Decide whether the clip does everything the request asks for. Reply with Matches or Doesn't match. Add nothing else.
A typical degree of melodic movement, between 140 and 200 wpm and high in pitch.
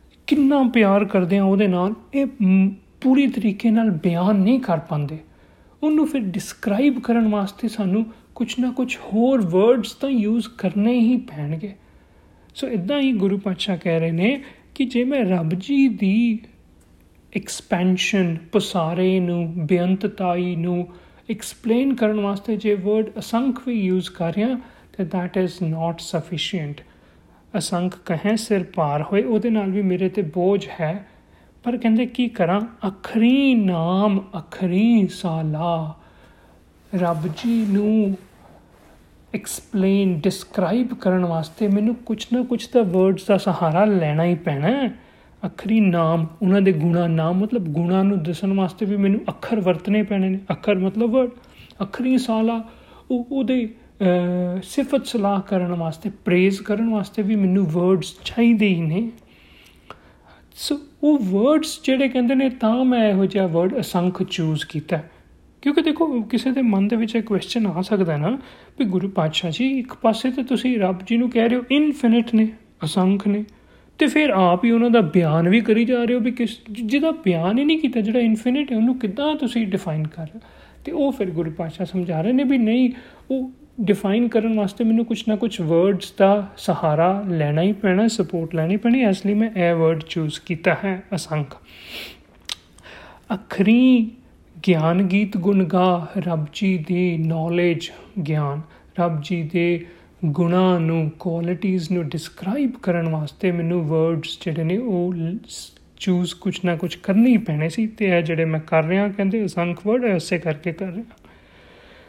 Matches